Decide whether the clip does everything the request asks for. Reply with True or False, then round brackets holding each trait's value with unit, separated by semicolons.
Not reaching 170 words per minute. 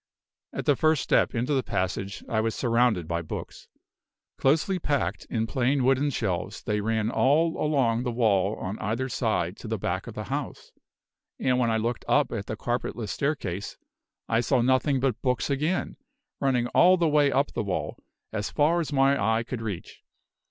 False (180 wpm)